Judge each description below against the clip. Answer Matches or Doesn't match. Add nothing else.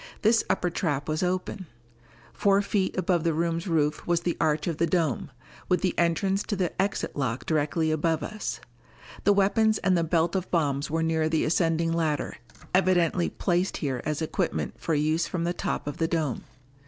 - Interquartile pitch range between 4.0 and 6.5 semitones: Doesn't match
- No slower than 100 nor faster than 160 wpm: Doesn't match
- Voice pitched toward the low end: Doesn't match